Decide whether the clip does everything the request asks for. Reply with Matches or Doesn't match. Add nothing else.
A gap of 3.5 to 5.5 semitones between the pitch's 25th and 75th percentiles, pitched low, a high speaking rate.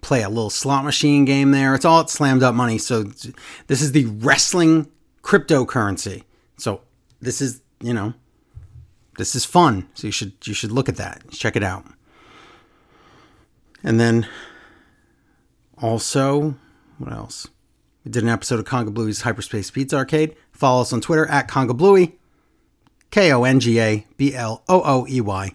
Doesn't match